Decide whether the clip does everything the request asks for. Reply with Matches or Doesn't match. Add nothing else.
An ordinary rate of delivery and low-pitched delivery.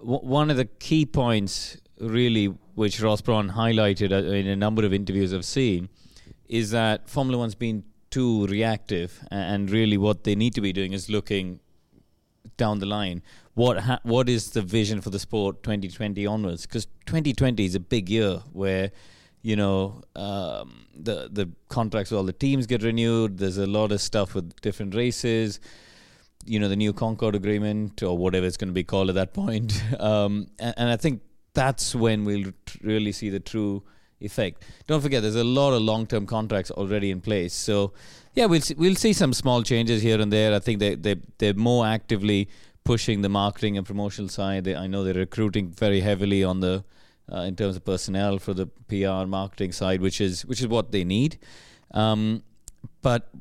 Matches